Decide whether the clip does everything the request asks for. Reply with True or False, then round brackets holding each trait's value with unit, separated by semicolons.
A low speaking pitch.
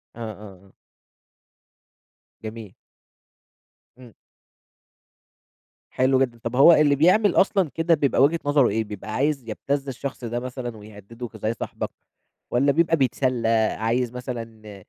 True (125 Hz)